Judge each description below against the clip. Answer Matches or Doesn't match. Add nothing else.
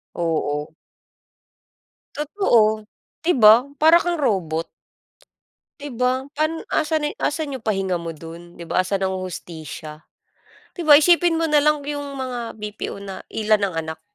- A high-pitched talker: Matches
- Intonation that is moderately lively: Doesn't match